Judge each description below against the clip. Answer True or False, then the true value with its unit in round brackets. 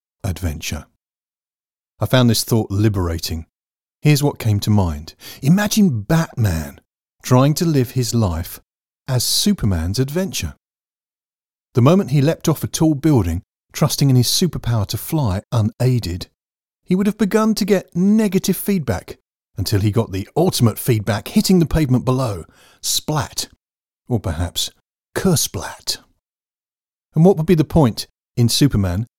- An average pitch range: False (8.3 semitones)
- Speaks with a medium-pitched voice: False (120 Hz)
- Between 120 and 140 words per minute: True (135 wpm)